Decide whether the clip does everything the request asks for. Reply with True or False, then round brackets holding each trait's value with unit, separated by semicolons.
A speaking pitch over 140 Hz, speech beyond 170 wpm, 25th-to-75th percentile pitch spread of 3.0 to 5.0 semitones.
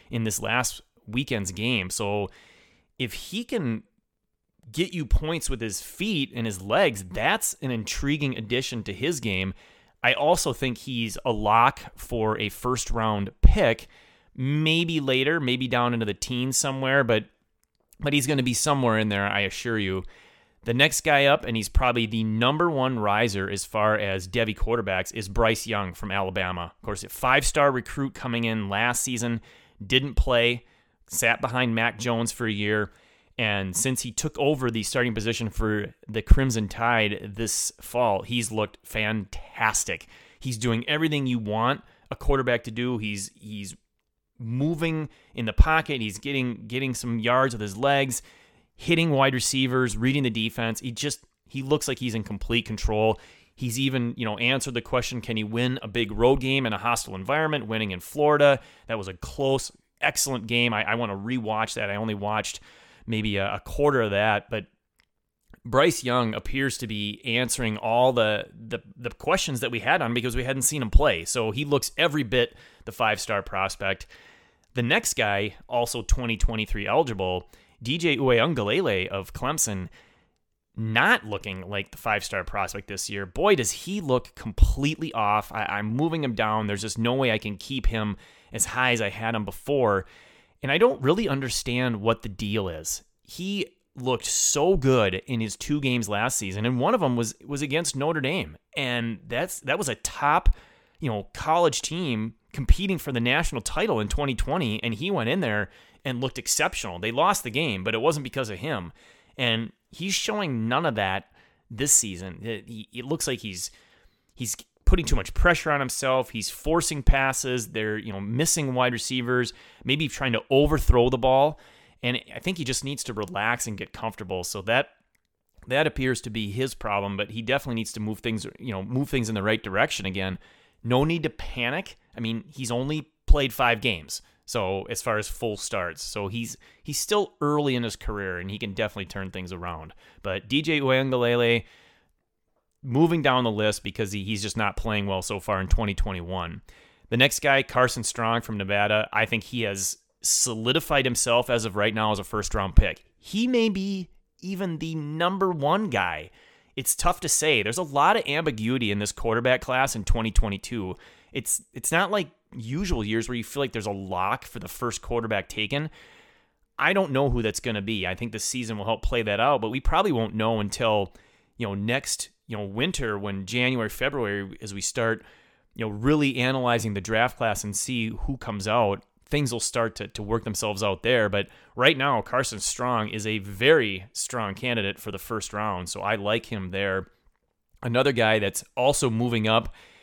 False (115 Hz; 185 wpm; 4.0 semitones)